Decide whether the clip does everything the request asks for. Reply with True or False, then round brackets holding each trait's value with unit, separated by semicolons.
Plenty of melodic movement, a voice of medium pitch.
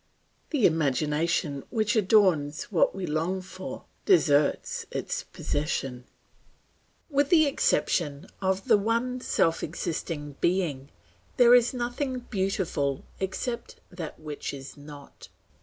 True (7.5 semitones; 180 Hz)